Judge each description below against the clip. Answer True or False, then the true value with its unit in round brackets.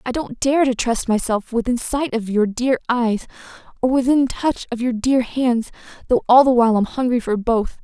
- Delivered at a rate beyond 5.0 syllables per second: False (4.9 syllables/s)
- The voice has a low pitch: False (245 Hz)